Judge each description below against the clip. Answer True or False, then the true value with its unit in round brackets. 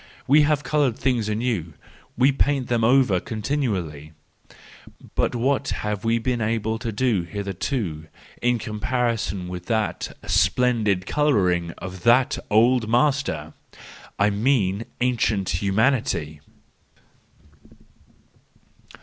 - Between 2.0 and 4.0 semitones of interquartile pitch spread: False (4.6 semitones)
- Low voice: True (110 Hz)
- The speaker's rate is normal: False (100 wpm)